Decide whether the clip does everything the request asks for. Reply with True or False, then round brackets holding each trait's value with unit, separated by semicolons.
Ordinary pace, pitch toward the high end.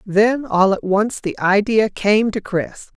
True (180 wpm; 210 Hz)